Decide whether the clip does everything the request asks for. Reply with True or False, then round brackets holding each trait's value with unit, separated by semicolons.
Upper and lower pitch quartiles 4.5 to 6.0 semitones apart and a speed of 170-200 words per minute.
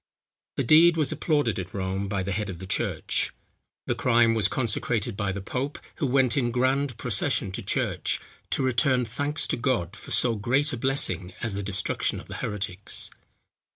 True (5.2 semitones; 185 wpm)